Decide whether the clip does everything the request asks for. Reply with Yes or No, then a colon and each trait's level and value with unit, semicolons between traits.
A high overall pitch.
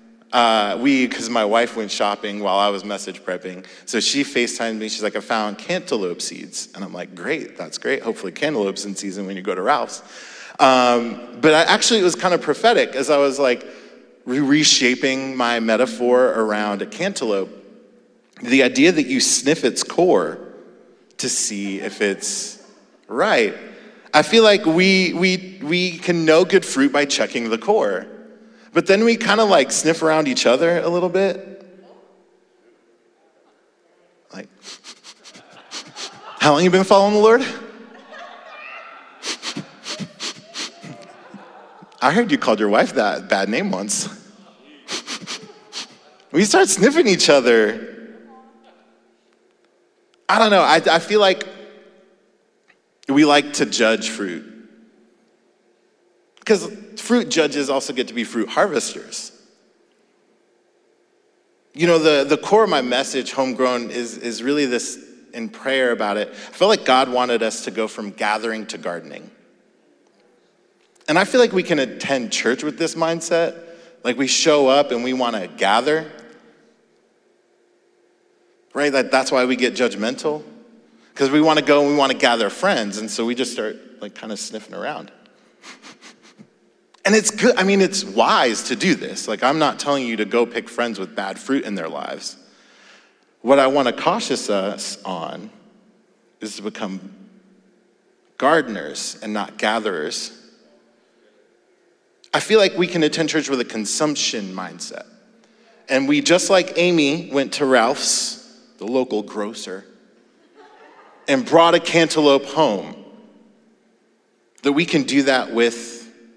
No: medium, 150 Hz